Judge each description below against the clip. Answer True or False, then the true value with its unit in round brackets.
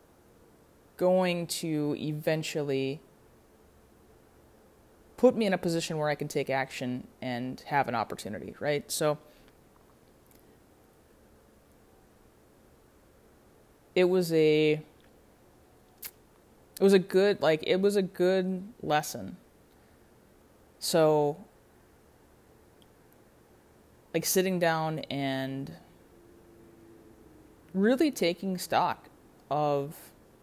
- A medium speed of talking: False (80 wpm)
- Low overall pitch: False (150 Hz)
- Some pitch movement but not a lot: False (6.4 semitones)